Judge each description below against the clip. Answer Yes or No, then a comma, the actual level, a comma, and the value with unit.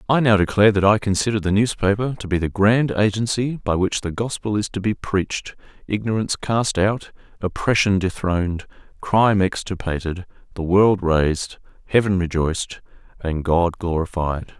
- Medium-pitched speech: No, low, 100 Hz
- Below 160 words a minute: Yes, average, 150 wpm